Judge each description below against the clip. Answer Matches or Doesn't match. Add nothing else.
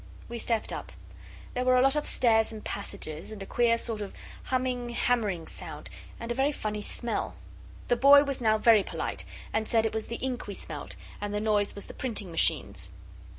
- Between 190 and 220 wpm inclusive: Matches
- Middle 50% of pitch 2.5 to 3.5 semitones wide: Matches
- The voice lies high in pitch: Matches